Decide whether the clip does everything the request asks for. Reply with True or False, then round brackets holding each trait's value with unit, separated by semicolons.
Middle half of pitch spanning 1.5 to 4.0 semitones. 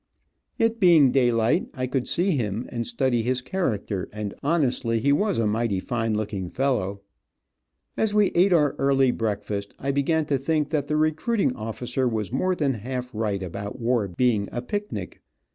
False (5.4 semitones)